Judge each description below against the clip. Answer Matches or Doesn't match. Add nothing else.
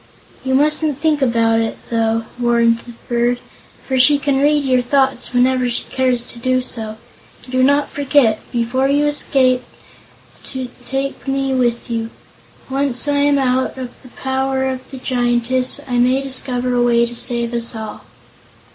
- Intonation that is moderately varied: Doesn't match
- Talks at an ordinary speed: Matches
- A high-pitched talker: Matches